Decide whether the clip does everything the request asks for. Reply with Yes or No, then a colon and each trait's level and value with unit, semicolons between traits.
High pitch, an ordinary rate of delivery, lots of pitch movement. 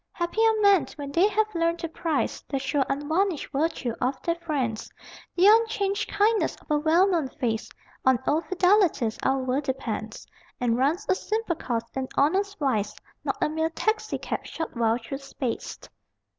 Yes: very high, 315 Hz; average, 170 wpm; wide, 6.5 semitones